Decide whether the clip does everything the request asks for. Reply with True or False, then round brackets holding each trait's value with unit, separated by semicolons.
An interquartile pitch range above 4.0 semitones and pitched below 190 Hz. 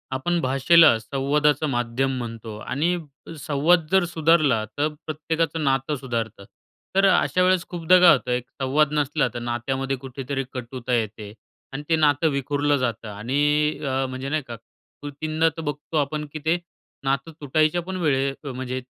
False (3.4 semitones; 140 Hz)